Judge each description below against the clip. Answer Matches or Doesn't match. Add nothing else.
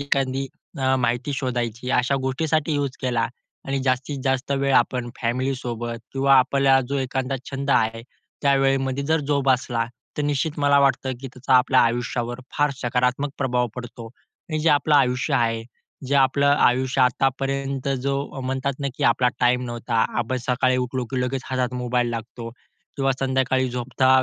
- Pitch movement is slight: Matches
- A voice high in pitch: Doesn't match